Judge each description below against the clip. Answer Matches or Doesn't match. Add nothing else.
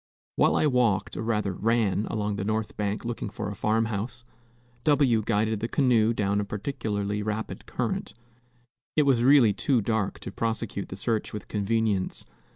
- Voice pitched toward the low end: Matches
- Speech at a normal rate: Matches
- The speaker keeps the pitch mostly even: Matches